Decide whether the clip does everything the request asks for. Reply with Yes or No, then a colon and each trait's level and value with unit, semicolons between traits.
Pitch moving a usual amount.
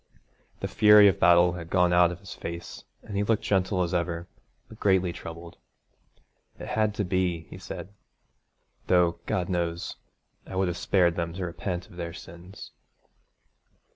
No: narrow, 1.9 semitones